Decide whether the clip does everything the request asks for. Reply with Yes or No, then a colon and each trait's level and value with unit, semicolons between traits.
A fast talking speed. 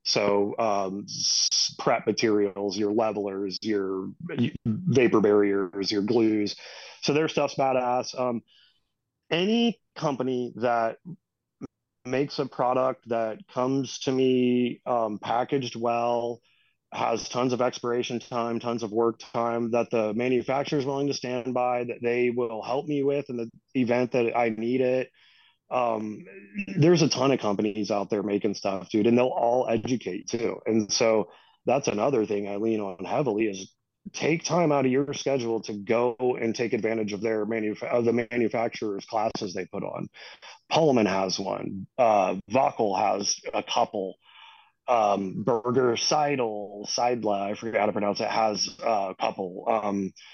No: average, 155 wpm